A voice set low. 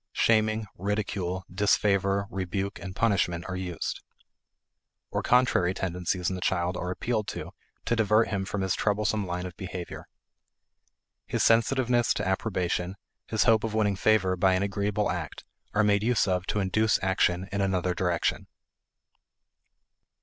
Yes: very low, 95 Hz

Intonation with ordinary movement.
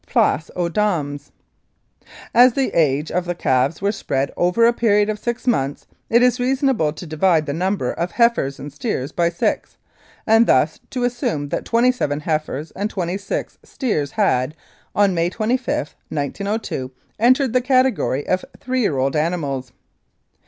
No: wide, 7.9 semitones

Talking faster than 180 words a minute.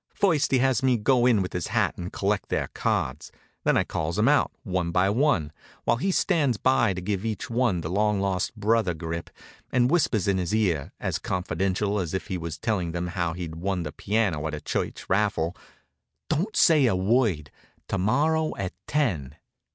Yes: average, 195 wpm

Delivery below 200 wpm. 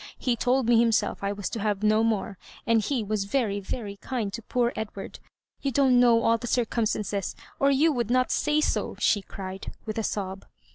No: fast, 205 wpm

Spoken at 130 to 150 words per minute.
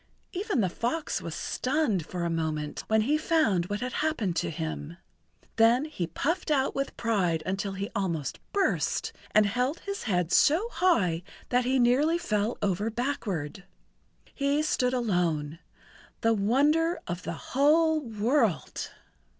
Yes: average, 140 wpm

